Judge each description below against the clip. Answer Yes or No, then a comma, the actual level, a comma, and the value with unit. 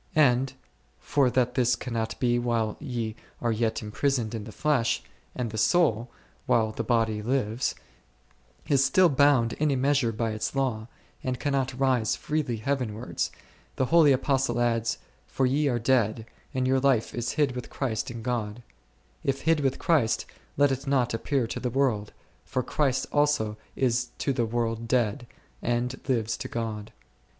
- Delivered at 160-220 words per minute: Yes, average, 165 wpm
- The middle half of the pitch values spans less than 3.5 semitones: Yes, average, 3.1 semitones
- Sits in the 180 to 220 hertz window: No, low, 125 Hz